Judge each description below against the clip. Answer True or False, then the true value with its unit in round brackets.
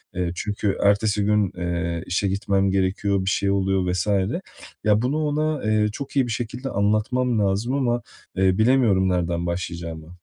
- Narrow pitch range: False (3.7 semitones)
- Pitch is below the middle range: True (100 Hz)